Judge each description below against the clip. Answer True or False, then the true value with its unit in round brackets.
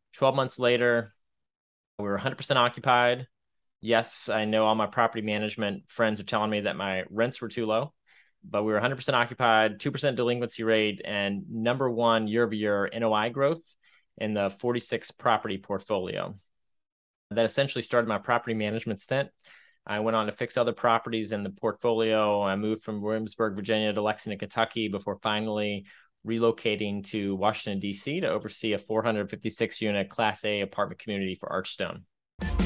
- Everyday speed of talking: True (155 wpm)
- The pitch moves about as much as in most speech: False (2.3 semitones)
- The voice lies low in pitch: True (110 Hz)